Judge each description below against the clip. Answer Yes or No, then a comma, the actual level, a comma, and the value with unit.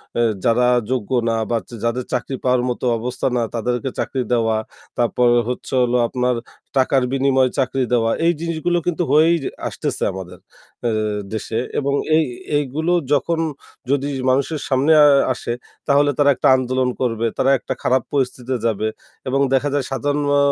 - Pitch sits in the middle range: No, low, 130 Hz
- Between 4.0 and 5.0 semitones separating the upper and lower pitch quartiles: No, average, 2.7 semitones